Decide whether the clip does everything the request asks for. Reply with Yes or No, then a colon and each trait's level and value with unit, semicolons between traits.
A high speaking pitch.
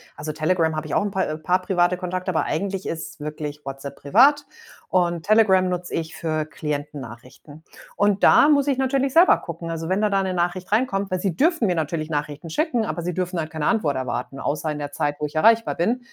No: medium, 175 Hz